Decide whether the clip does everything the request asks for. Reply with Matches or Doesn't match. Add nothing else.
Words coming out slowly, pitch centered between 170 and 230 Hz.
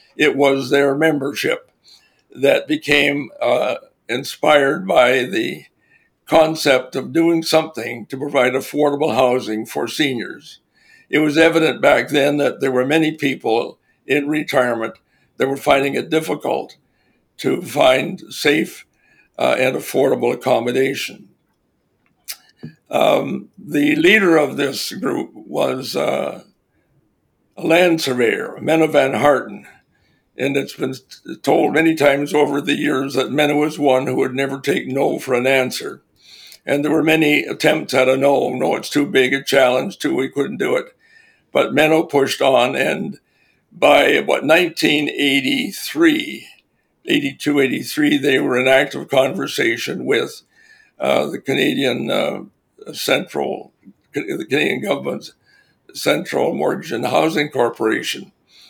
Doesn't match